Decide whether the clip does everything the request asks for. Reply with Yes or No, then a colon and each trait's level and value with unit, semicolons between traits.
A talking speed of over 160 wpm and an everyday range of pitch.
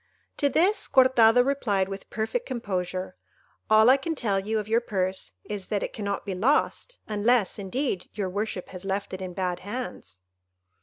Yes: average, 170 wpm; average, 4.5 semitones